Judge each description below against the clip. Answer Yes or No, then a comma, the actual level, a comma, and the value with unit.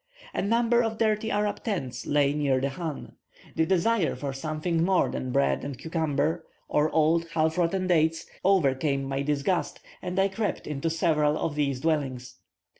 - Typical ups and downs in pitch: Yes, average, 4.6 semitones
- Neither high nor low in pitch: Yes, medium, 160 Hz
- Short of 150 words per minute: No, average, 165 wpm